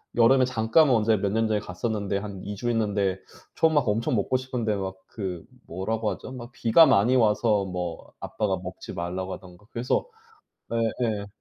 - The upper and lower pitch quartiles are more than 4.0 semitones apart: No, average, 3.5 semitones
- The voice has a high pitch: No, low, 105 Hz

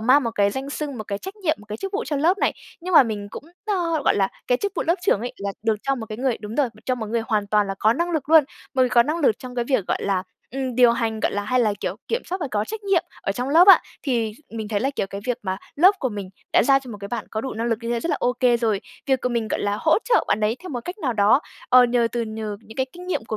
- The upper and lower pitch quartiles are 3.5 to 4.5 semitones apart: No, average, 5.2 semitones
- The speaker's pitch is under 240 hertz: No, high, 245 Hz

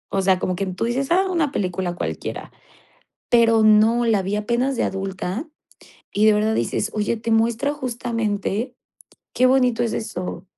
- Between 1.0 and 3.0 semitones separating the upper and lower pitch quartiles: No, average, 3.5 semitones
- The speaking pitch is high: Yes, high, 220 Hz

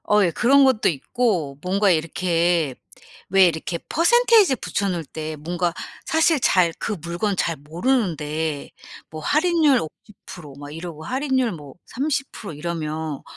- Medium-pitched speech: Yes, medium, 175 Hz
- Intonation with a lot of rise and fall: Yes, wide, 7.8 semitones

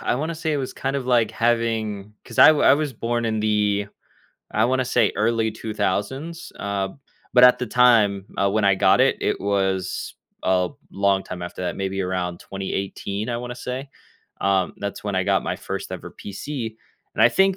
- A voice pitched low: Yes, low, 110 Hz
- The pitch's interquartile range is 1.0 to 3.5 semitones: No, average, 4.1 semitones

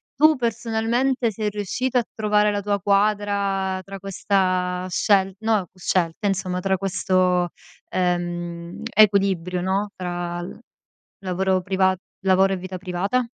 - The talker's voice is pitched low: No, high, 190 Hz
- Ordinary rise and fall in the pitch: No, narrow, 2.3 semitones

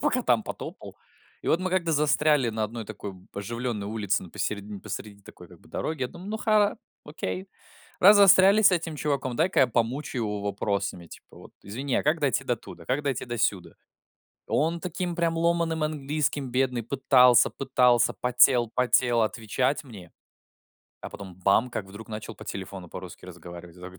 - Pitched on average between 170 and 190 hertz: No, low, 125 Hz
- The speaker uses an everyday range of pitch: No, wide, 6.6 semitones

